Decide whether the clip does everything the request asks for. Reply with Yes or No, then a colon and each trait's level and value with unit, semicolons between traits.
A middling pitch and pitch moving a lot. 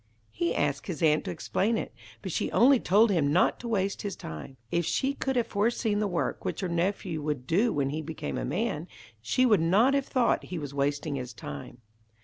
Yes: medium, 175 Hz; wide, 7.1 semitones